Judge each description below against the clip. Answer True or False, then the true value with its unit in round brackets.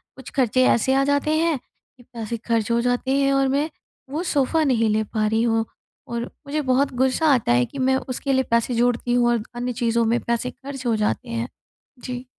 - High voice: True (245 Hz)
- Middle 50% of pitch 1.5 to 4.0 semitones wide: True (2.8 semitones)